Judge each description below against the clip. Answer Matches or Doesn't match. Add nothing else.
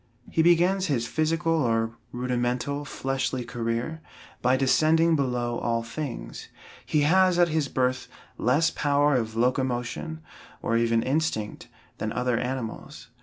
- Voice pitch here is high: Doesn't match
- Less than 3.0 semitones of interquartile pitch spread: Doesn't match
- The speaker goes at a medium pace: Doesn't match